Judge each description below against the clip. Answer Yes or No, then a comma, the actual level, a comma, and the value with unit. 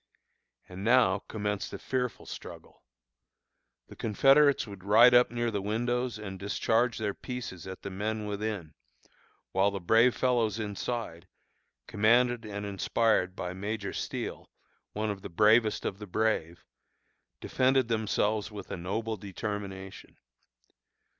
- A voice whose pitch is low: Yes, low, 105 Hz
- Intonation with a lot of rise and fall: No, average, 2.9 semitones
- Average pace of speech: No, slow, 130 wpm